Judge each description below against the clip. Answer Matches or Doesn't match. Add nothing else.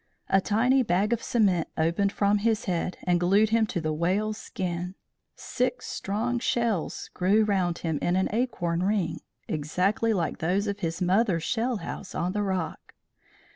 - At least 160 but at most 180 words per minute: Matches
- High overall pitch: Matches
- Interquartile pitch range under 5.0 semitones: Matches